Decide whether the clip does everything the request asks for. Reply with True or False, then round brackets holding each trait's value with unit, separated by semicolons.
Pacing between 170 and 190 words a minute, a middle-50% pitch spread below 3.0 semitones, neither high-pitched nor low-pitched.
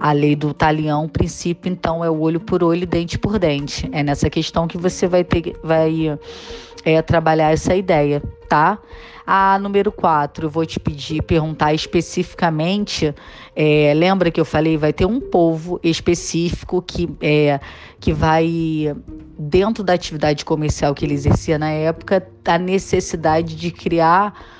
False (160 wpm; 2.6 semitones; 160 Hz)